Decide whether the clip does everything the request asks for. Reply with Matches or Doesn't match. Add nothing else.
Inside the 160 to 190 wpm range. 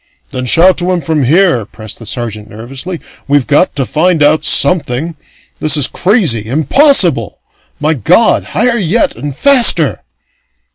Doesn't match